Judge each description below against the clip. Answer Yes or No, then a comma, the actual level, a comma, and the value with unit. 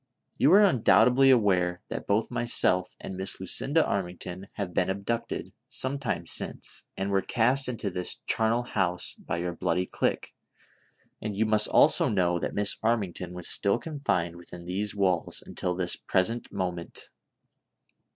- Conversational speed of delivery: Yes, average, 150 wpm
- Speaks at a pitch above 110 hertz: No, low, 100 Hz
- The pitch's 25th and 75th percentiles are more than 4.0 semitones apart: Yes, average, 4.5 semitones